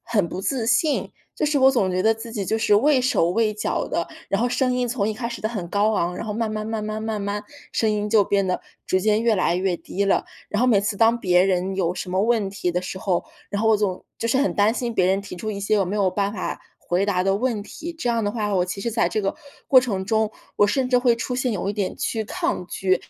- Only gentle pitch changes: No, average, 3.2 semitones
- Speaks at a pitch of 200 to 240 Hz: Yes, high, 210 Hz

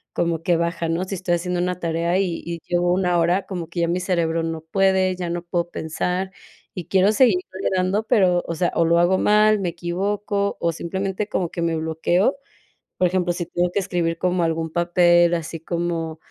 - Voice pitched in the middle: Yes, medium, 175 Hz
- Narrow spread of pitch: Yes, narrow, 1.8 semitones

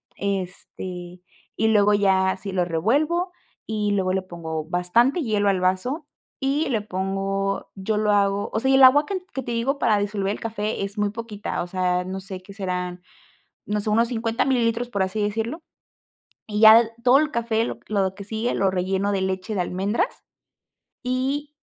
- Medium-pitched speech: No, high, 205 Hz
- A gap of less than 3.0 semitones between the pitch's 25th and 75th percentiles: No, average, 3.5 semitones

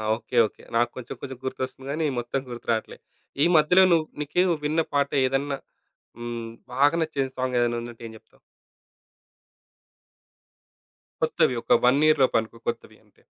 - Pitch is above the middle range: No, low, 130 Hz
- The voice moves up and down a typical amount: Yes, average, 3.6 semitones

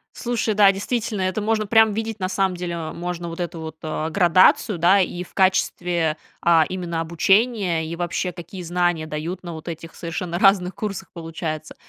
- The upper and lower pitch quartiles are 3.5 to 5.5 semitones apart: No, average, 2.8 semitones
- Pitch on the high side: No, medium, 180 Hz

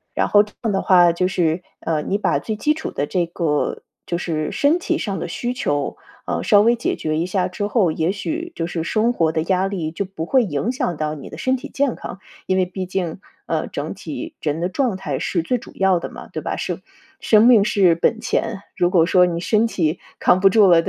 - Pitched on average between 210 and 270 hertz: No, medium, 185 Hz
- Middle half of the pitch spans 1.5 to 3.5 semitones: No, average, 4.4 semitones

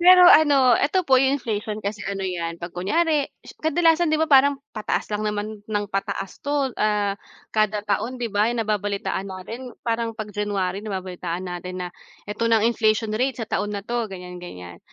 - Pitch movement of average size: Yes, average, 4.5 semitones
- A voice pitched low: No, high, 215 Hz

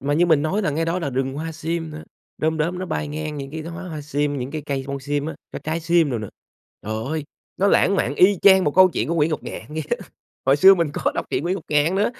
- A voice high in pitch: No, medium, 155 Hz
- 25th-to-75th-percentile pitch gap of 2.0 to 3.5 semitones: Yes, average, 2.8 semitones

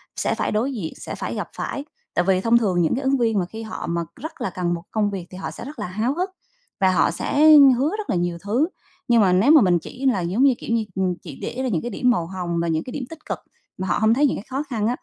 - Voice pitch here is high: Yes, high, 215 Hz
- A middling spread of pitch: No, wide, 6.2 semitones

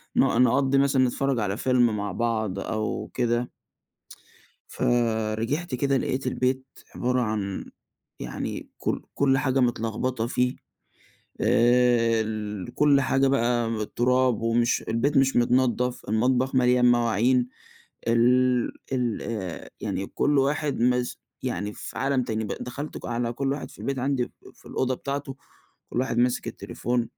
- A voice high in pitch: No, low, 125 Hz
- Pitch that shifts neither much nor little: No, narrow, 2.3 semitones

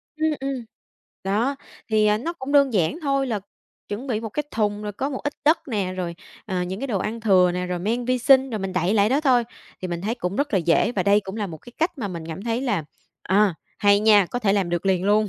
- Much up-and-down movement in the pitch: No, average, 5.0 semitones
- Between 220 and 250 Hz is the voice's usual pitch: No, high, 210 Hz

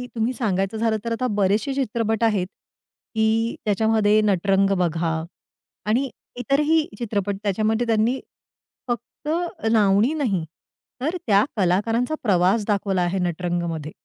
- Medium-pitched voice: No, high, 215 Hz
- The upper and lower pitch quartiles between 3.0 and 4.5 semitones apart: Yes, average, 3.3 semitones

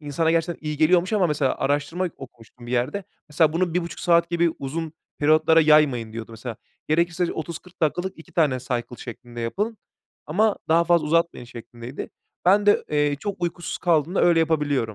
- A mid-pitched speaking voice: Yes, medium, 155 Hz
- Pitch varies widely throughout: No, average, 4.2 semitones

